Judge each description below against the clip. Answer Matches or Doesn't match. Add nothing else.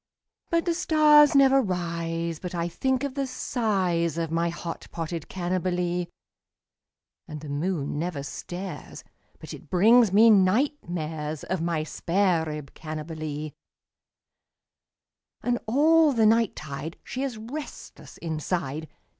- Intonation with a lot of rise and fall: Matches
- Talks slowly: Matches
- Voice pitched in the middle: Matches